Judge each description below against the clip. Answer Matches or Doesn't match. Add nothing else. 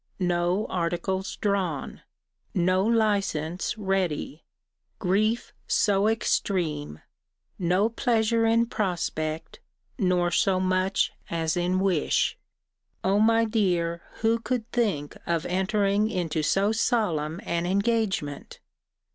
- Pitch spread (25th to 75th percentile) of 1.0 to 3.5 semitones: Doesn't match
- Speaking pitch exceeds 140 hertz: Matches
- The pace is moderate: Doesn't match